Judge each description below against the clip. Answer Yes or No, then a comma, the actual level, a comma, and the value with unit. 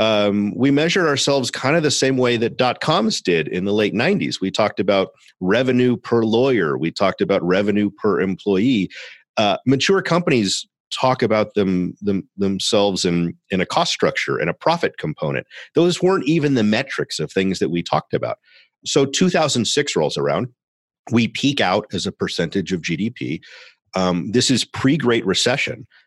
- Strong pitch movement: Yes, wide, 5.7 semitones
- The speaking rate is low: No, average, 175 wpm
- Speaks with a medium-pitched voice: No, low, 115 Hz